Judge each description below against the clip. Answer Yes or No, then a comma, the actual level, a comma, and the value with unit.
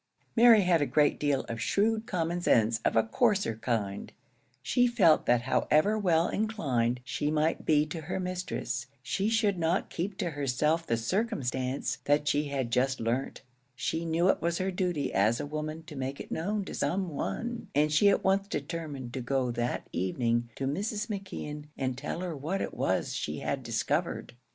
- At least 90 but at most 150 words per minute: No, average, 185 wpm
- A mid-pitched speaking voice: Yes, medium, 155 Hz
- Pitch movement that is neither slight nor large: No, wide, 6.4 semitones